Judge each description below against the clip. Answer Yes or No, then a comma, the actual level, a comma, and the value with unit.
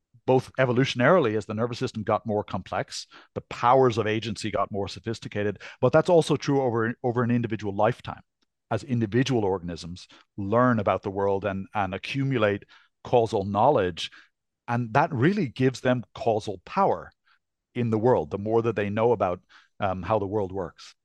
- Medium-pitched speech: No, low, 115 Hz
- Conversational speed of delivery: Yes, average, 165 wpm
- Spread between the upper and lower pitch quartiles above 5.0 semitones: No, average, 3.5 semitones